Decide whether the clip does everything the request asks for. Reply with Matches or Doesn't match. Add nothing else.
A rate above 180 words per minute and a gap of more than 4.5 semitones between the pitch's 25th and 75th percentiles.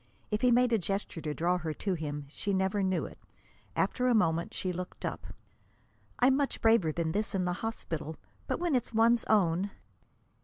Matches